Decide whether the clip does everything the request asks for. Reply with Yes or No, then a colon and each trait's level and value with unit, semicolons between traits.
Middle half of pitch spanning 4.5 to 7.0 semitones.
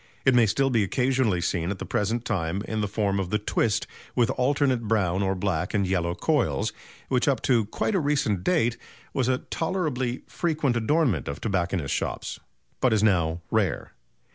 Yes: average, 5.2 semitones